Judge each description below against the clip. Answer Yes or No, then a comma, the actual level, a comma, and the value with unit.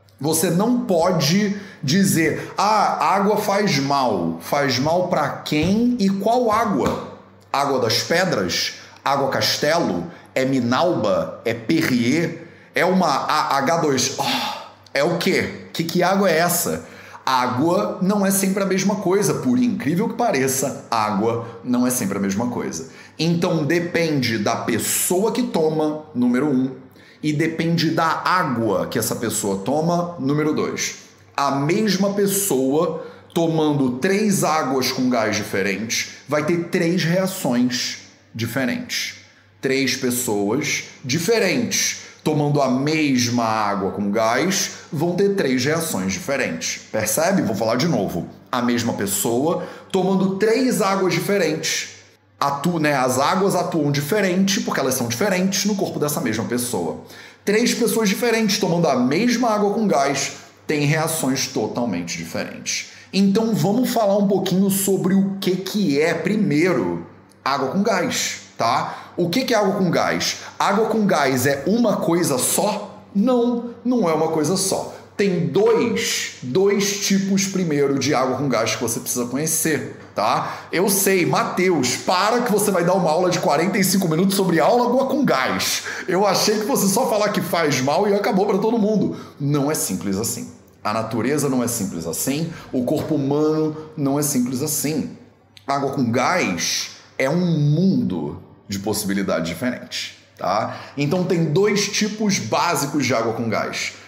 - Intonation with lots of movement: Yes, wide, 7.1 semitones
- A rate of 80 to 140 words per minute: No, average, 150 wpm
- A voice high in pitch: No, medium, 165 Hz